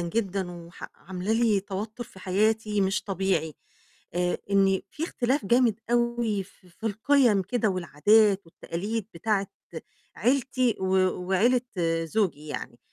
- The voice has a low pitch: No, high, 200 Hz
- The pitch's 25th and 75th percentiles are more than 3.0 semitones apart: Yes, average, 3.7 semitones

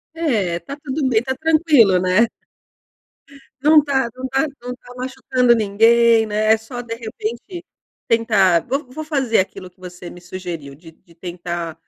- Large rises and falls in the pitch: Yes, wide, 6.1 semitones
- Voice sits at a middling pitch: No, high, 230 Hz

